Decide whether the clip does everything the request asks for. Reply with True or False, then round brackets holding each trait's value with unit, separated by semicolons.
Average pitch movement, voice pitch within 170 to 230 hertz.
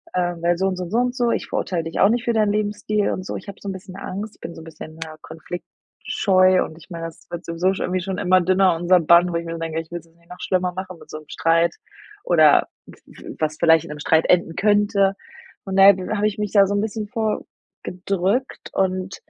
True (3.1 semitones; 185 Hz)